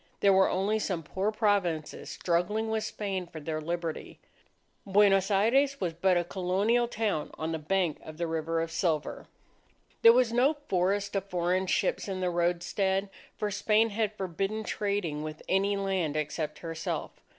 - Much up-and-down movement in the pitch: No, average, 3.5 semitones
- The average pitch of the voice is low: No, high, 190 Hz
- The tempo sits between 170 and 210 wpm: No, average, 160 wpm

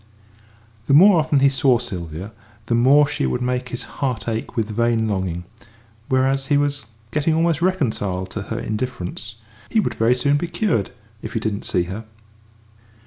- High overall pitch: No, low, 125 Hz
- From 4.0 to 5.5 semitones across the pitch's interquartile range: Yes, average, 4.9 semitones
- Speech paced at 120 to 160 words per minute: No, average, 170 wpm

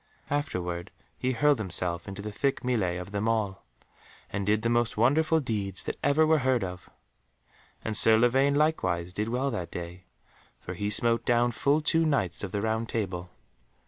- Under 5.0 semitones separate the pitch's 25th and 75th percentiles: No, wide, 5.6 semitones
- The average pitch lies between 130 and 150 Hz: No, low, 110 Hz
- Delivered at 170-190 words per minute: Yes, average, 175 wpm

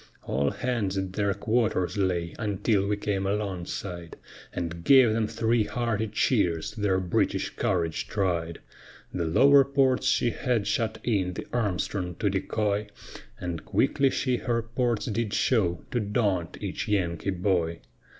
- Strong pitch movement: No, average, 4.3 semitones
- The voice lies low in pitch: Yes, low, 100 Hz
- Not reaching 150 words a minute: Yes, average, 140 wpm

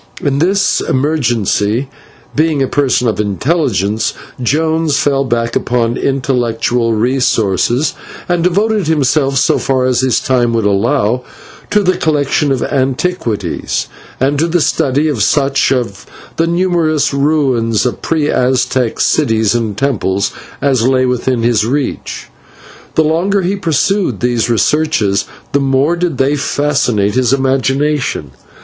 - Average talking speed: No, slow, 130 wpm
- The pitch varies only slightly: No, average, 4.3 semitones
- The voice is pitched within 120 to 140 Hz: Yes, low, 135 Hz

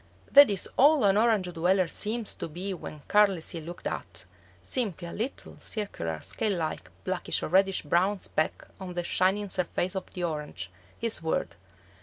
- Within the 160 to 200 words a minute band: Yes, average, 165 wpm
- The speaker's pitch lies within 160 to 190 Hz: Yes, medium, 185 Hz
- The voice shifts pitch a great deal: No, average, 3.6 semitones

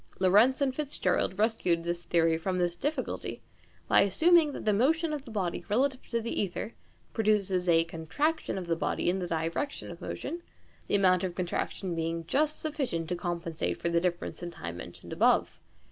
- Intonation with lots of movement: Yes, wide, 7.1 semitones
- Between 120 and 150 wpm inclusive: No, average, 180 wpm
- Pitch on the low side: No, medium, 185 Hz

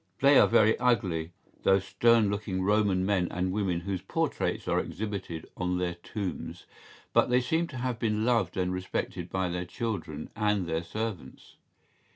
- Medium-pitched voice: No, very low, 95 Hz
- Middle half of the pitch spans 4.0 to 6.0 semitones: No, average, 3.6 semitones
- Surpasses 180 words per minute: No, average, 170 wpm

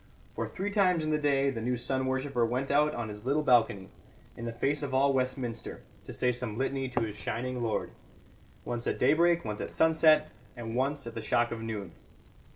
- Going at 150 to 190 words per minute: No, fast, 205 wpm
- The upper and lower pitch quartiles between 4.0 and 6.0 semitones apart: No, average, 3.6 semitones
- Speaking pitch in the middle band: No, low, 130 Hz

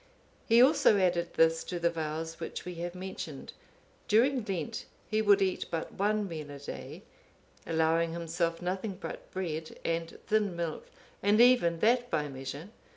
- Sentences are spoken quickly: No, average, 155 wpm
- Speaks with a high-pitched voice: No, medium, 175 Hz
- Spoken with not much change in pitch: No, average, 4.0 semitones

